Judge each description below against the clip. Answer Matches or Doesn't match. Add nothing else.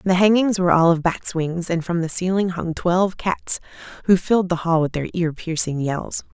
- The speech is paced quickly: Matches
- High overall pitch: Doesn't match